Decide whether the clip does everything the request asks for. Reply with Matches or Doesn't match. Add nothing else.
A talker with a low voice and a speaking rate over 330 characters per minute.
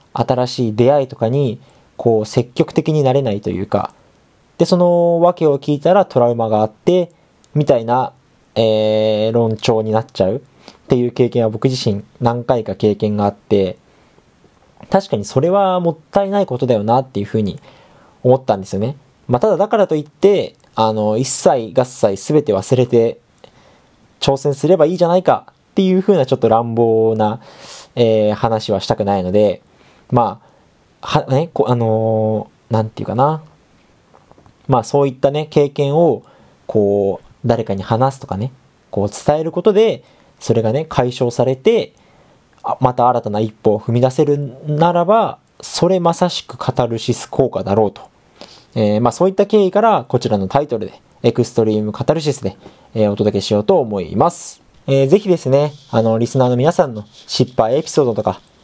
Doesn't match